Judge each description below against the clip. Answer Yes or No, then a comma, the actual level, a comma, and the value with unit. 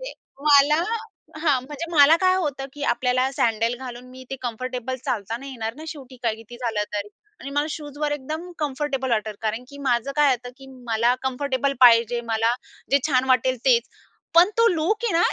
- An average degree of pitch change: Yes, average, 3.5 semitones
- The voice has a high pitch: Yes, very high, 260 Hz